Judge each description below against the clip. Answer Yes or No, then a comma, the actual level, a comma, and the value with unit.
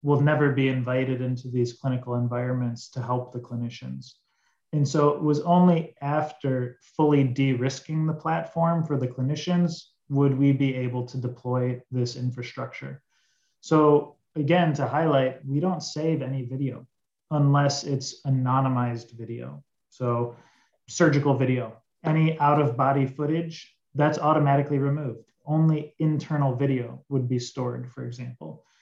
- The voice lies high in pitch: No, low, 135 Hz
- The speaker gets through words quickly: No, slow, 135 wpm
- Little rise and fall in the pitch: No, average, 3.2 semitones